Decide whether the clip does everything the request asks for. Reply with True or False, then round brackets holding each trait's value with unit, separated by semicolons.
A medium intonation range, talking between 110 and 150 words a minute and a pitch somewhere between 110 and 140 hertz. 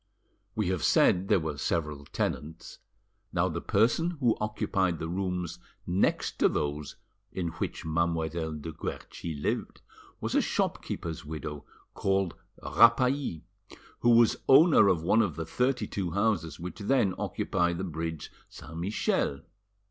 False (4.8 semitones; 140 wpm; 90 Hz)